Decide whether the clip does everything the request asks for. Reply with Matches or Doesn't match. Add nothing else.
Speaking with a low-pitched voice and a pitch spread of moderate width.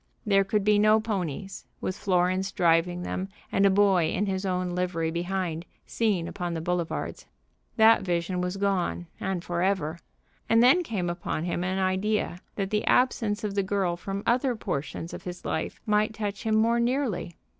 Doesn't match